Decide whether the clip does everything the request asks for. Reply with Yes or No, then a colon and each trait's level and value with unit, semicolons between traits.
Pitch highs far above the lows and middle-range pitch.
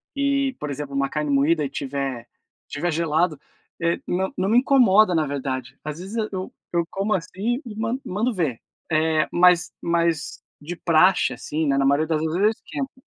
No: average, 4.8 semitones; medium, 170 Hz